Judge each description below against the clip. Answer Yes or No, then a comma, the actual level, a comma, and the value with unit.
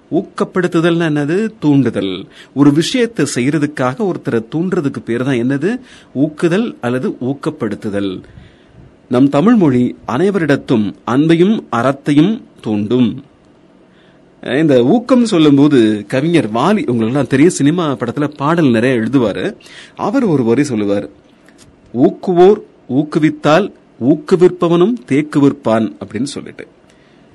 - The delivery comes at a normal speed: Yes, average, 90 wpm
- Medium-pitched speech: Yes, medium, 145 Hz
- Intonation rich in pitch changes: Yes, wide, 6.0 semitones